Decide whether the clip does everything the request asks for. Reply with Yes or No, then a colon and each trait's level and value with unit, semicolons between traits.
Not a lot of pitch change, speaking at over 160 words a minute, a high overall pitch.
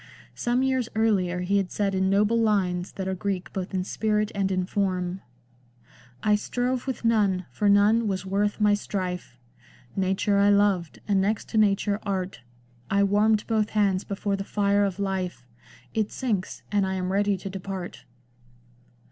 Yes: narrow, 1.9 semitones; average, 175 wpm; high, 200 Hz